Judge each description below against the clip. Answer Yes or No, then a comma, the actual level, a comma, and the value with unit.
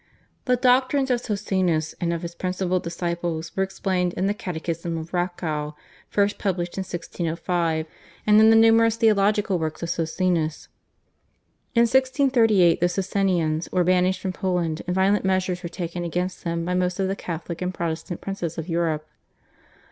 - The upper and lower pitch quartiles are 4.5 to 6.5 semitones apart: No, average, 2.7 semitones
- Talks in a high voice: No, medium, 180 Hz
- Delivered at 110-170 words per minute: Yes, average, 160 wpm